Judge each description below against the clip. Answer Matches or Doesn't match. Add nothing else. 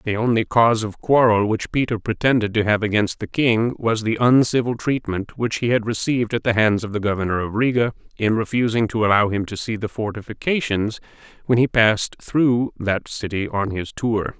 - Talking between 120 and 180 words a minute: Doesn't match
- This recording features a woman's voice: Doesn't match